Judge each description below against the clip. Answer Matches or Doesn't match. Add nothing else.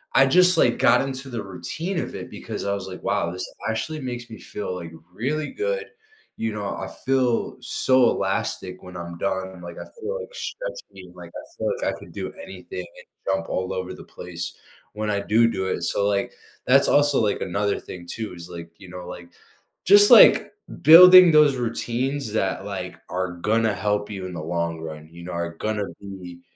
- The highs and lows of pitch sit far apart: Matches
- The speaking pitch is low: Matches